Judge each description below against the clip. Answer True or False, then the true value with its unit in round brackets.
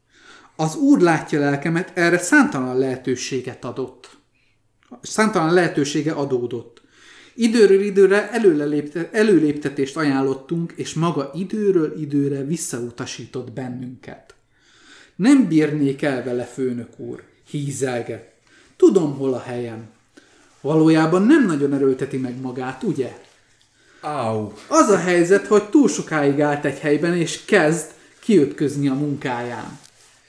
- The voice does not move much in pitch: False (4.8 semitones)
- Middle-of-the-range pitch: True (145 Hz)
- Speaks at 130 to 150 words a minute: False (105 wpm)